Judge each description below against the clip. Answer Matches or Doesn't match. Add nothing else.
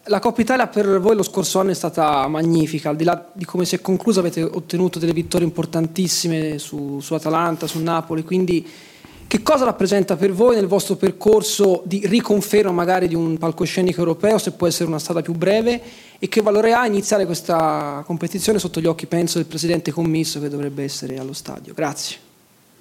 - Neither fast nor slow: Doesn't match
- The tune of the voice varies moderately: Matches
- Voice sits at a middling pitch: Matches